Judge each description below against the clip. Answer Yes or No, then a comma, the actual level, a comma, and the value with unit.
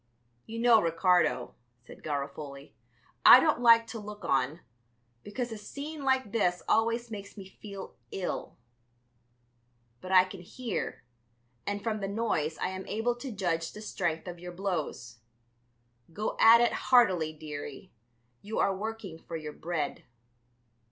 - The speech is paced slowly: No, average, 145 wpm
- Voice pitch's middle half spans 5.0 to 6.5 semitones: Yes, wide, 5.4 semitones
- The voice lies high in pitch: Yes, high, 195 Hz